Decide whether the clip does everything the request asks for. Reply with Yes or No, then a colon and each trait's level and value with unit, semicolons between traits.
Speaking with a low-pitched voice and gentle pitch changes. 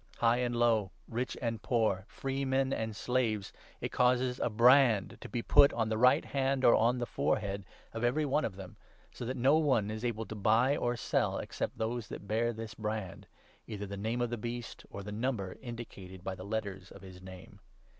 No: low, 115 Hz; average, 3.3 semitones